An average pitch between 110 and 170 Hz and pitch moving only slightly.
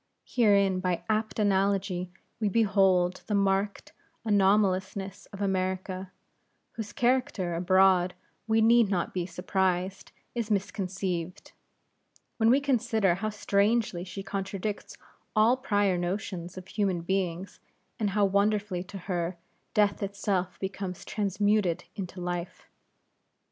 No: high, 195 Hz; narrow, 2.2 semitones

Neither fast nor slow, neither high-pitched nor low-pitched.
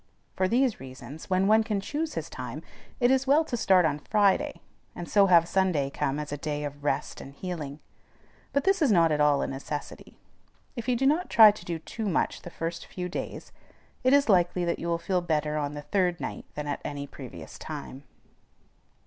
No: fast, 210 wpm; medium, 175 Hz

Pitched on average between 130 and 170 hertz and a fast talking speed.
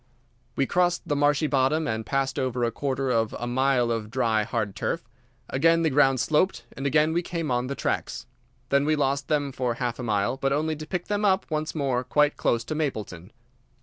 Yes: low, 135 Hz; fast, 210 wpm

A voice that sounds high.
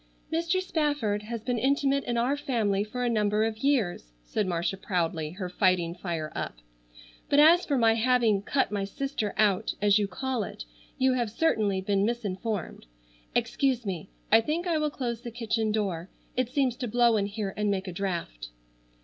Yes: high, 220 Hz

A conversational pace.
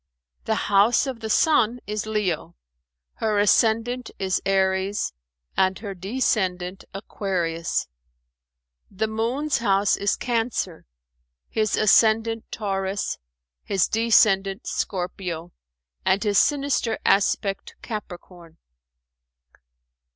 No: slow, 90 wpm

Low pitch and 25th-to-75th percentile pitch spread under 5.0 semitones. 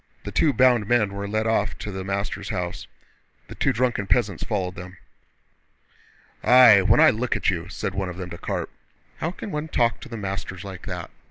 Yes: low, 100 Hz; average, 4.1 semitones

